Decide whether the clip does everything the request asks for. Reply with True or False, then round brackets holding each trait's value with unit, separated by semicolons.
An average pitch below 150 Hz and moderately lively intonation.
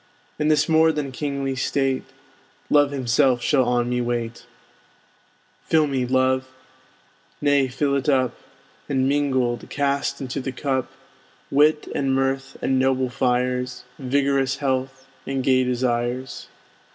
False (135 Hz; 1.7 semitones)